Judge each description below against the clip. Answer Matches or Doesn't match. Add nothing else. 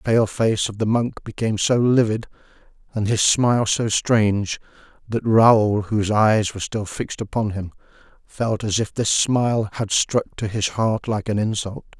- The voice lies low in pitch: Matches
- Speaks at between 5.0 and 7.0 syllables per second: Doesn't match